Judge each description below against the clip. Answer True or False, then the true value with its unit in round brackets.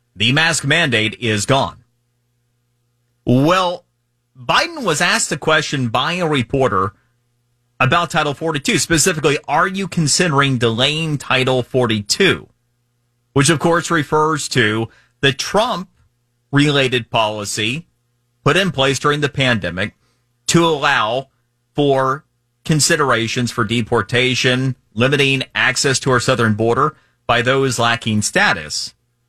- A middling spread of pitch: True (3.5 semitones)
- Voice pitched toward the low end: True (125 Hz)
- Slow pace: True (115 wpm)